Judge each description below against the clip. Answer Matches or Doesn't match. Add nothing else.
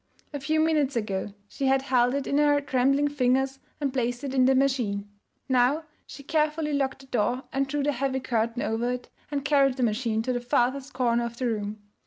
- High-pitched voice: Matches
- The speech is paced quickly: Matches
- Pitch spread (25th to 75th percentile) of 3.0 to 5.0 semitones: Doesn't match